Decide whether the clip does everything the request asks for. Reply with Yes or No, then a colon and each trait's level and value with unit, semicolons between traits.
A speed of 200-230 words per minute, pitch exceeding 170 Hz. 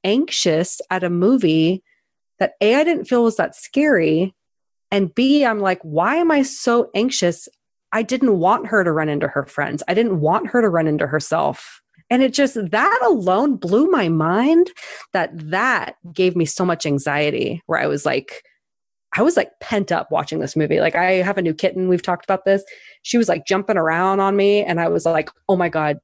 Yes: fast, 205 wpm; high, 190 Hz